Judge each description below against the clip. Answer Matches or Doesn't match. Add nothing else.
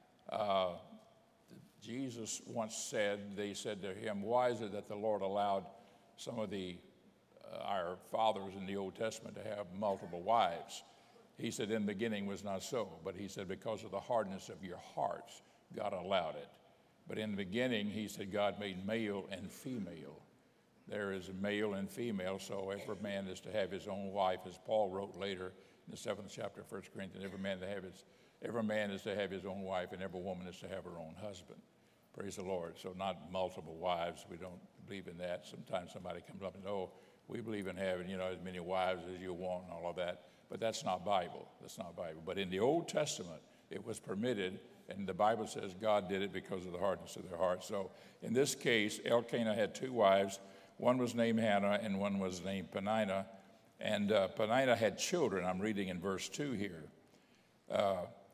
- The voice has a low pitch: Matches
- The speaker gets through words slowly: Doesn't match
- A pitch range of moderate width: Doesn't match